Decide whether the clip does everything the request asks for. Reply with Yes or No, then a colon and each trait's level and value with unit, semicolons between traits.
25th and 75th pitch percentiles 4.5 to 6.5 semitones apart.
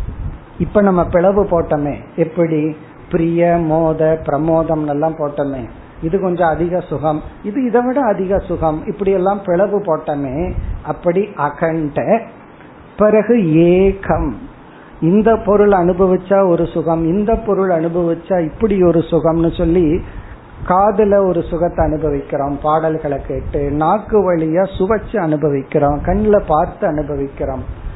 No: average, 4.1 semitones